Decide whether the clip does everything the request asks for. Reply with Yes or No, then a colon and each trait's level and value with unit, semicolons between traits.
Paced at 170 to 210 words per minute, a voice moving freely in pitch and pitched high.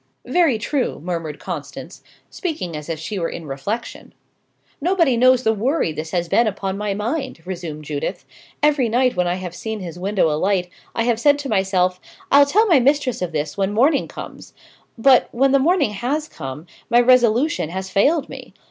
Yes: average, 185 wpm; wide, 7.1 semitones; high, 215 Hz